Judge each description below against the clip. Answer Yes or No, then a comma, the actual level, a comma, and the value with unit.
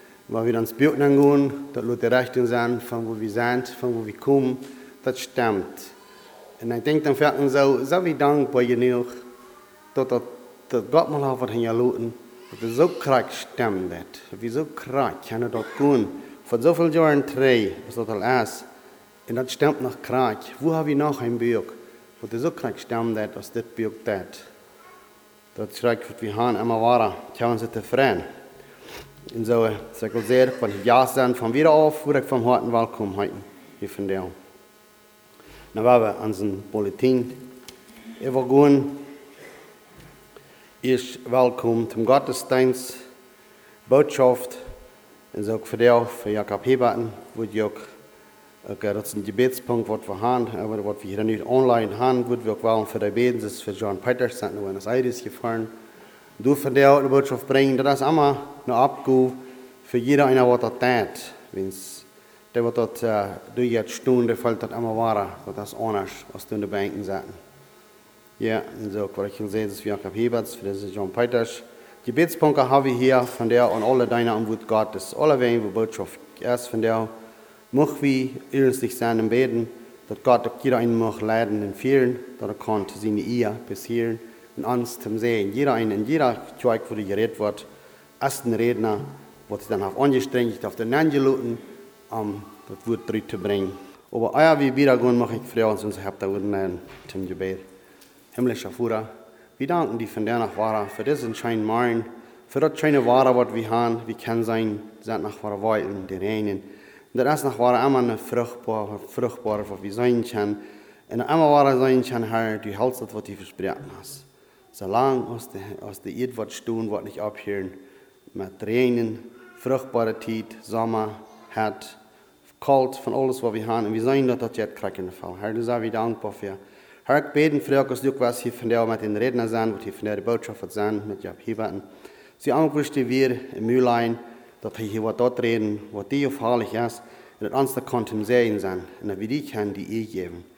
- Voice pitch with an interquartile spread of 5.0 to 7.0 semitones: No, average, 3.0 semitones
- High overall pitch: No, low, 120 Hz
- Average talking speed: Yes, average, 165 wpm